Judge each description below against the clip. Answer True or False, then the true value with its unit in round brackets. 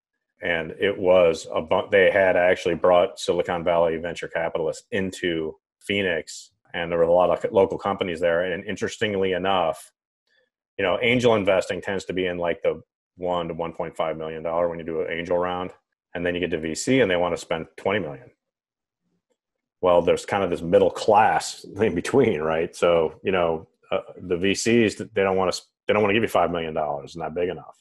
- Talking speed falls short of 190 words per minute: False (205 wpm)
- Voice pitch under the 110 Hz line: True (95 Hz)